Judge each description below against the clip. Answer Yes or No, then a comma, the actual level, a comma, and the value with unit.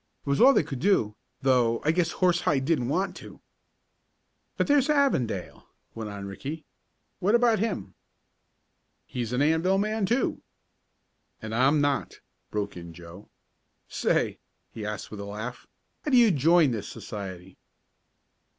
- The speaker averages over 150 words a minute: No, average, 145 wpm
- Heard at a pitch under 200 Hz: Yes, medium, 140 Hz